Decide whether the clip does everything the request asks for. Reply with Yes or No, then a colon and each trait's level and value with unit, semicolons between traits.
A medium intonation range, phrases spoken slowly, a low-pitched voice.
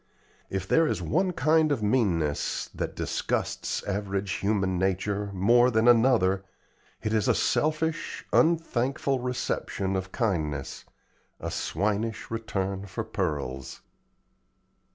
Yes: average, 4.6 semitones; slow, 110 wpm; low, 105 Hz